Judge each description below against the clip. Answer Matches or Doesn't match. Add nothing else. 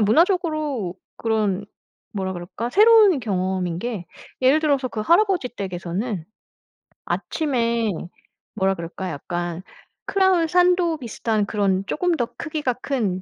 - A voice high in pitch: Matches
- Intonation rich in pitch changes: Matches